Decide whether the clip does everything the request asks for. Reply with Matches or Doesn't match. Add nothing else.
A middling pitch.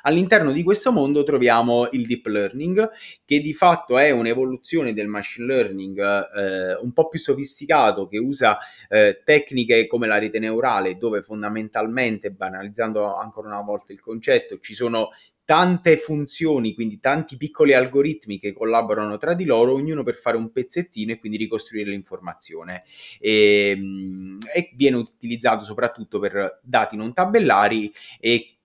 Doesn't match